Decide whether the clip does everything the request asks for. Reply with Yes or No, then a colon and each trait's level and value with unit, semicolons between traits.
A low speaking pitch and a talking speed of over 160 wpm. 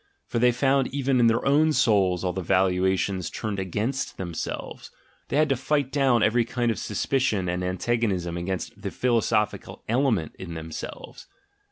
Yes: low, 110 Hz; average, 170 wpm